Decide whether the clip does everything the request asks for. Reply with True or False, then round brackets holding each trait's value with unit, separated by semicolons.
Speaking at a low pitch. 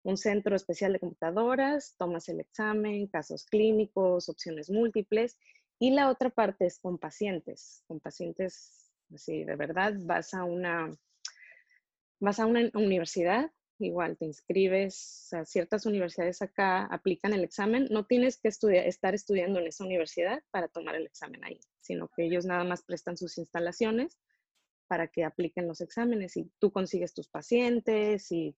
False (190 Hz)